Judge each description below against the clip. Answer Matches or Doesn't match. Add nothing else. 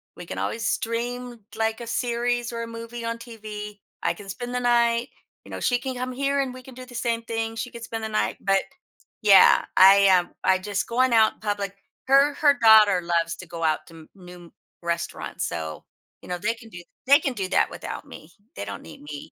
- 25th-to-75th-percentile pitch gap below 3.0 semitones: Doesn't match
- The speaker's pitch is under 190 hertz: Doesn't match